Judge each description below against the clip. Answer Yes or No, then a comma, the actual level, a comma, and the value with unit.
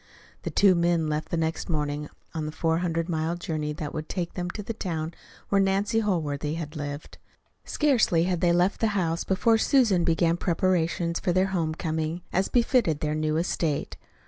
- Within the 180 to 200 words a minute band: Yes, average, 185 wpm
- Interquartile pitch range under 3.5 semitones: Yes, average, 3.0 semitones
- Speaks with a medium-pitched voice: Yes, medium, 170 Hz